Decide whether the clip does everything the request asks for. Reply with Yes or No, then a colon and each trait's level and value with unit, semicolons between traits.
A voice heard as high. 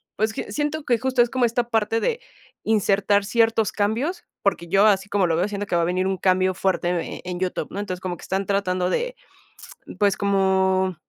Yes: high, 200 Hz